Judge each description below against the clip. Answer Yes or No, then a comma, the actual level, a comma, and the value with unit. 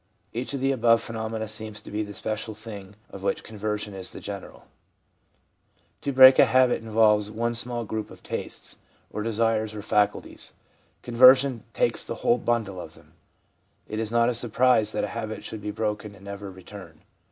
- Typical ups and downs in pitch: No, narrow, 2.1 semitones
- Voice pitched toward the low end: Yes, low, 110 Hz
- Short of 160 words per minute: No, average, 180 wpm